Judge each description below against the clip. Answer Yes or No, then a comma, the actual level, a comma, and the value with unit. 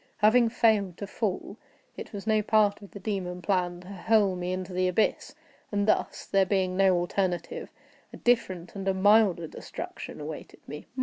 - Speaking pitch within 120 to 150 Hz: No, high, 195 Hz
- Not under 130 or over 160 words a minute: No, average, 175 wpm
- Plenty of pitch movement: No, narrow, 2.6 semitones